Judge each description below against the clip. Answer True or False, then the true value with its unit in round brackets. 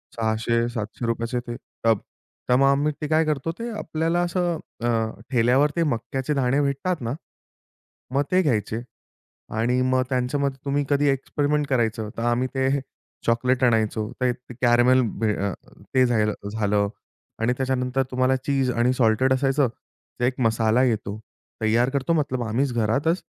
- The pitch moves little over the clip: False (3.2 semitones)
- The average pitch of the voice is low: True (125 Hz)